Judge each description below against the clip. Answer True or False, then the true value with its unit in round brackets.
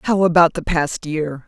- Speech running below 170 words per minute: False (205 wpm)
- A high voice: False (165 Hz)